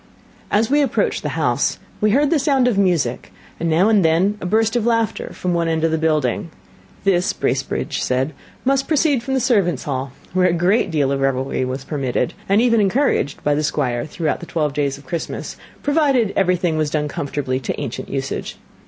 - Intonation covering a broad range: Yes, wide, 7.6 semitones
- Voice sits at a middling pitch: Yes, medium, 170 Hz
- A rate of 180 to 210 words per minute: Yes, average, 195 wpm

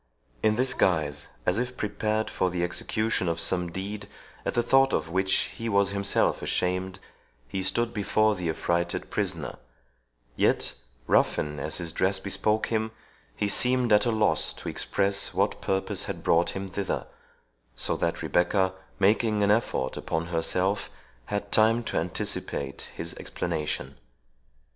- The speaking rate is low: No, average, 150 wpm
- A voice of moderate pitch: No, low, 100 Hz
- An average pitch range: Yes, average, 3.7 semitones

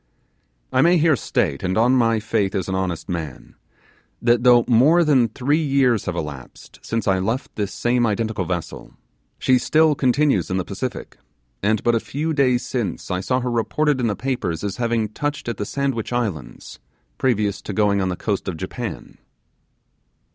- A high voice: No, low, 115 Hz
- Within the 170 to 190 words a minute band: Yes, average, 180 wpm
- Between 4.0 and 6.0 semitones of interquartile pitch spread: Yes, average, 4.9 semitones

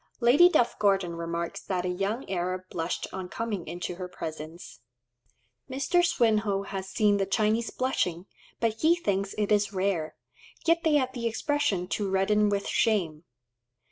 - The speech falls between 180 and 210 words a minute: No, average, 155 wpm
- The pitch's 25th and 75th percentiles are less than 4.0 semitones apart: No, average, 4.3 semitones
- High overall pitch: Yes, high, 200 Hz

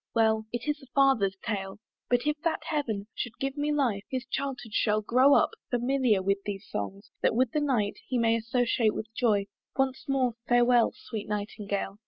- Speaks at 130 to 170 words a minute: No, average, 180 wpm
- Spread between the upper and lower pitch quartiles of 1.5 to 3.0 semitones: No, average, 4.3 semitones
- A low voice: No, high, 240 Hz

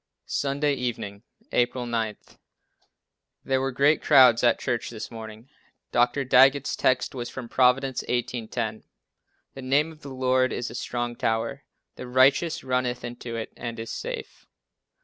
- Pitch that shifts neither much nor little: No, narrow, 2.2 semitones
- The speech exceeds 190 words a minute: No, average, 150 wpm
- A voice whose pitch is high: No, low, 125 Hz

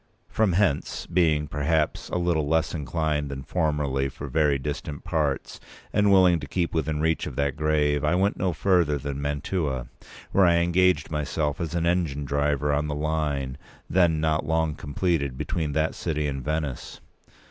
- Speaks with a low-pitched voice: Yes, very low, 75 Hz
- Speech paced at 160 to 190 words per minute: Yes, average, 170 wpm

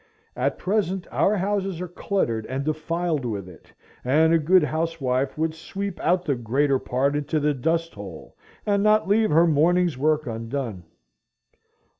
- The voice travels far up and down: No, average, 5.0 semitones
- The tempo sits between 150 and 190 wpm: Yes, average, 155 wpm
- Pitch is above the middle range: No, medium, 155 Hz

